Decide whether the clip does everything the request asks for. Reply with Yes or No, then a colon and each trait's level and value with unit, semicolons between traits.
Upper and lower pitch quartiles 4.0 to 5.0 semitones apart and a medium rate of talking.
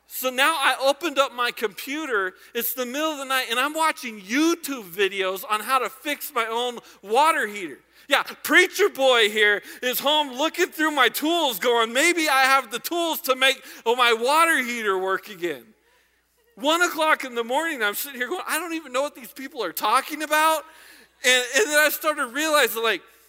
Yes: average, 4.5 semitones; average, 195 wpm